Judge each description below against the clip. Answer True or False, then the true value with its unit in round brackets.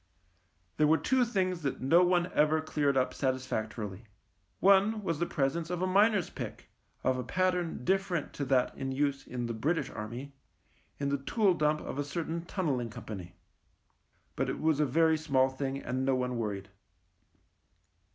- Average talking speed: True (170 wpm)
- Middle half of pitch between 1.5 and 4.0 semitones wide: False (5.2 semitones)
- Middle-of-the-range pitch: True (145 Hz)